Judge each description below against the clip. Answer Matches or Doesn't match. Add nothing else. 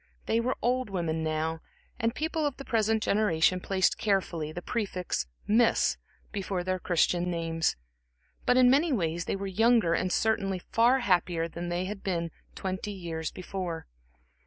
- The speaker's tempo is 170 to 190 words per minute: Doesn't match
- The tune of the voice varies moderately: Matches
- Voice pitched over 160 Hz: Matches